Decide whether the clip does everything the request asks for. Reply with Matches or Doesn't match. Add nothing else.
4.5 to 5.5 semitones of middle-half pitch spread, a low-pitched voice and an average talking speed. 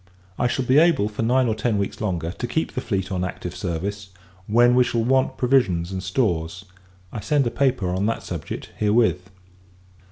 Matches